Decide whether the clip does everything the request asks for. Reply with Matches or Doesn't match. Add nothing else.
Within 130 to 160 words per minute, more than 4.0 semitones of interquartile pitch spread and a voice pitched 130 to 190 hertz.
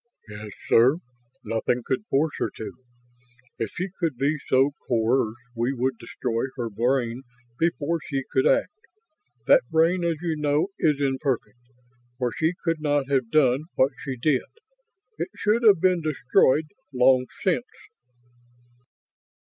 Matches